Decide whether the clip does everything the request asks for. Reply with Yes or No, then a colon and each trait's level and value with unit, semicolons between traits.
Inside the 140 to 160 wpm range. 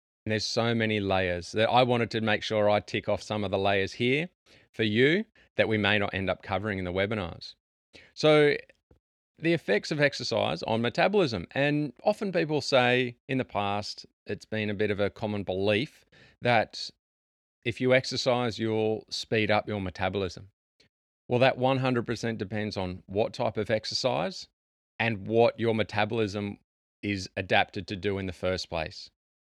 No: average, 170 wpm